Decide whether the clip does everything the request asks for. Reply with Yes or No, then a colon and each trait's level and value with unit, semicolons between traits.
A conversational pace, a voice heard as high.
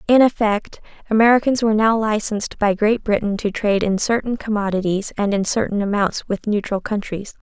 Yes: average, 170 wpm; high, 210 Hz